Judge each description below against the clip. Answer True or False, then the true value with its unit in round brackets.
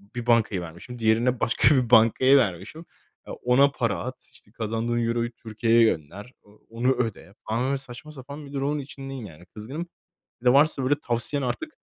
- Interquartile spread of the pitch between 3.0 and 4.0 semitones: True (3.3 semitones)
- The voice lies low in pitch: True (120 Hz)